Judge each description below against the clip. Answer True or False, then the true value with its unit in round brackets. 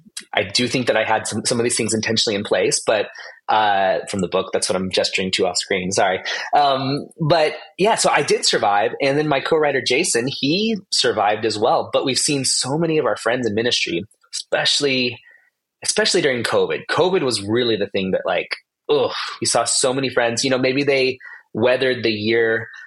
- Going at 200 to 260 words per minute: True (205 wpm)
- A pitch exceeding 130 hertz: True (140 Hz)